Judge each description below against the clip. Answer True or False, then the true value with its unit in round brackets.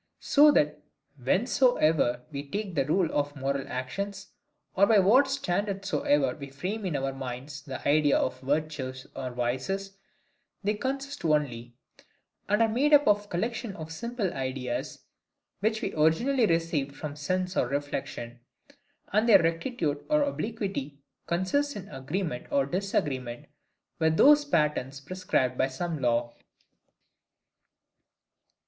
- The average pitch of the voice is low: False (160 Hz)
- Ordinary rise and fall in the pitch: False (7.1 semitones)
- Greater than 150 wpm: False (135 wpm)